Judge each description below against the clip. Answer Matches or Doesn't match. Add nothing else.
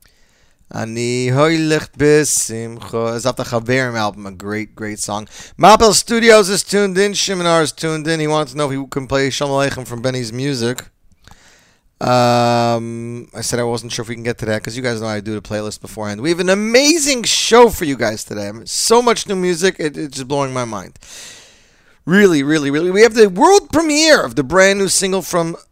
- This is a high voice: Doesn't match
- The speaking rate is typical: Matches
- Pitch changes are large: Matches